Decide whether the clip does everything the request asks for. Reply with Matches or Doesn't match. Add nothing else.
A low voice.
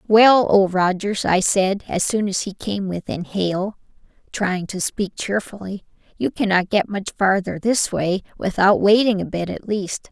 Doesn't match